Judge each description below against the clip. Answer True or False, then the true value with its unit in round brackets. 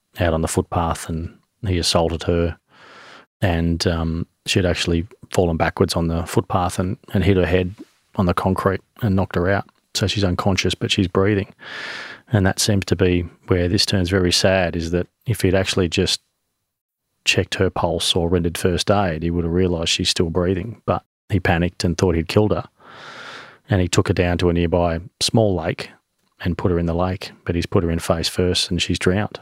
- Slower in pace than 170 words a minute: False (200 wpm)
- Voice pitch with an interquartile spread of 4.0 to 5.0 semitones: False (2.4 semitones)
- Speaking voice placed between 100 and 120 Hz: False (90 Hz)